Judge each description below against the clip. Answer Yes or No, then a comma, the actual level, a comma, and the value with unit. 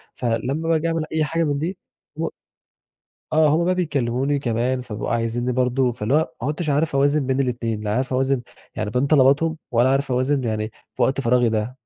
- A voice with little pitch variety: No, average, 3.8 semitones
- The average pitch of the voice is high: No, low, 135 Hz